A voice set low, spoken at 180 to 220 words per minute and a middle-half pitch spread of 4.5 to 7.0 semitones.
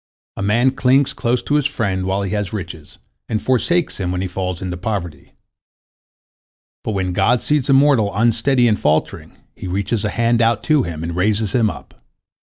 Yes: low, 105 Hz; average, 185 wpm; average, 4.8 semitones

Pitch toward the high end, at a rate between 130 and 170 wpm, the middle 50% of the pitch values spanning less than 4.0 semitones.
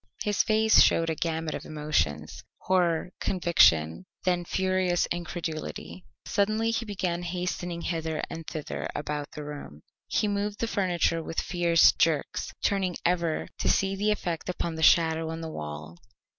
No: medium, 170 Hz; average, 150 wpm; average, 3.1 semitones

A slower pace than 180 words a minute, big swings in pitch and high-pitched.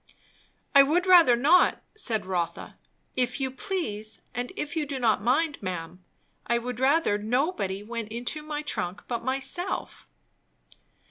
Yes: average, 140 wpm; wide, 6.0 semitones; very high, 250 Hz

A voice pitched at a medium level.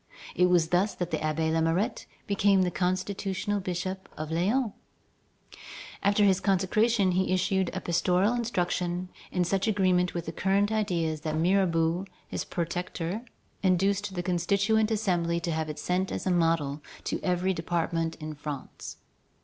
Yes: medium, 180 Hz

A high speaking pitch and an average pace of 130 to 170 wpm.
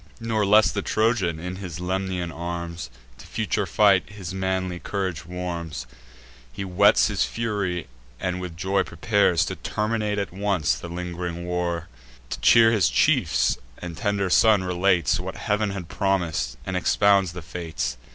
No: very low, 90 Hz; average, 150 wpm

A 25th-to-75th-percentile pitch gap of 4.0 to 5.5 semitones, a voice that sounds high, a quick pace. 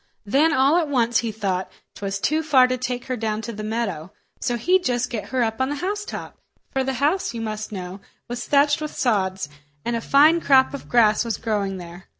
Yes: average, 4.7 semitones; high, 240 Hz; fast, 210 wpm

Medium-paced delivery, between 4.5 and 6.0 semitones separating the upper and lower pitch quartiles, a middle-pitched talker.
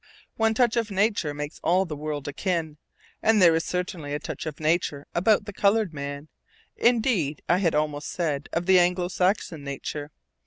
Yes: average, 170 wpm; average, 4.9 semitones; medium, 170 Hz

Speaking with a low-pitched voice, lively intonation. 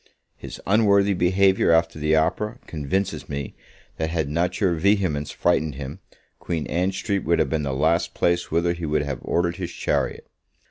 No: very low, 85 Hz; average, 3.5 semitones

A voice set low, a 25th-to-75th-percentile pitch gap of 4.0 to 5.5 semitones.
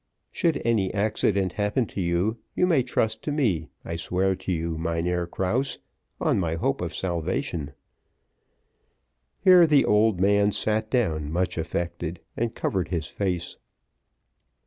Yes: very low, 95 Hz; average, 4.4 semitones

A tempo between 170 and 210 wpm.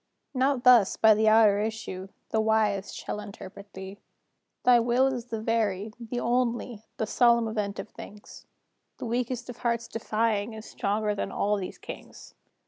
No: average, 160 wpm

